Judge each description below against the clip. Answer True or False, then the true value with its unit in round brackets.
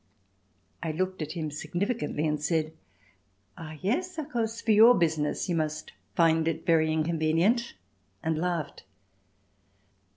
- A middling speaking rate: False (130 wpm)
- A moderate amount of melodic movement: True (4.4 semitones)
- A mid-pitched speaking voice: True (165 Hz)